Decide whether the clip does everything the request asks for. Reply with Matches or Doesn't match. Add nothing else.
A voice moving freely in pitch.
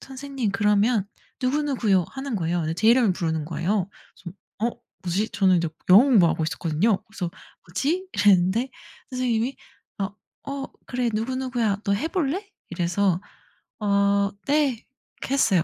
Matches